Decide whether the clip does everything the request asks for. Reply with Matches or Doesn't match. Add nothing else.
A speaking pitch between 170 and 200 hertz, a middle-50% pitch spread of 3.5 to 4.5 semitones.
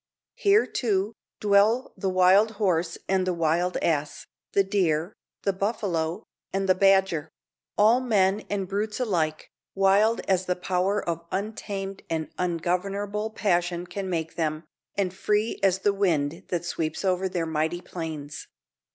Doesn't match